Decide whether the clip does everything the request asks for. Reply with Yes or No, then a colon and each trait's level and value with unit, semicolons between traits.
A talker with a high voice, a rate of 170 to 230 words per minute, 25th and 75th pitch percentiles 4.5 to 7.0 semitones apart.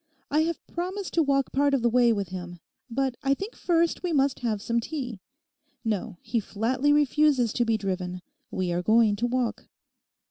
Yes: high, 245 Hz; average, 185 wpm; average, 5.3 semitones